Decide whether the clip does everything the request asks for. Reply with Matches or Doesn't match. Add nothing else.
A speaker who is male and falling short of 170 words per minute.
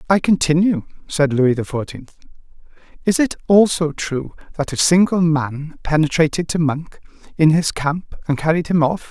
Matches